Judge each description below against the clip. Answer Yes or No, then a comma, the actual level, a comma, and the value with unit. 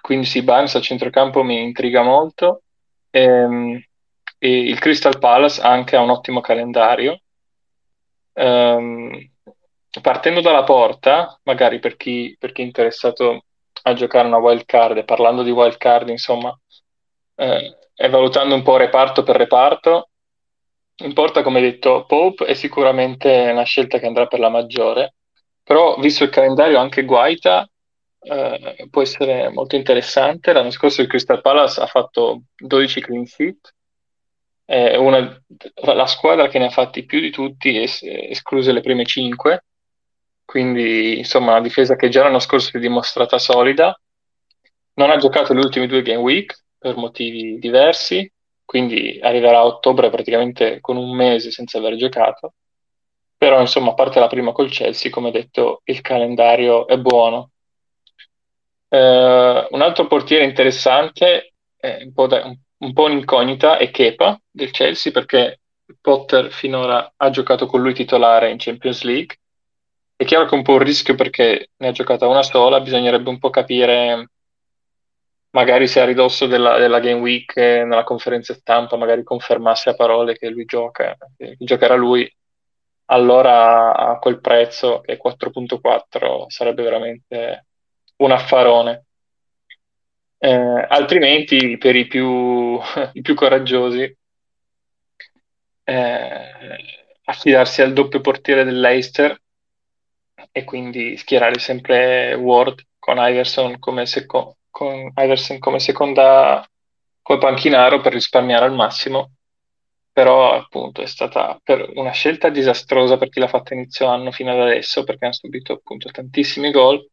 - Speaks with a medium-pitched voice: No, low, 125 Hz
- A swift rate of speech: No, average, 145 wpm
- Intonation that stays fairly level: Yes, narrow, 2.1 semitones